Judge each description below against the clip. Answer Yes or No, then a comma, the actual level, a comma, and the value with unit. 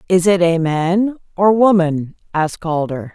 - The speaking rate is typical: Yes, average, 155 wpm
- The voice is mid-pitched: Yes, medium, 175 Hz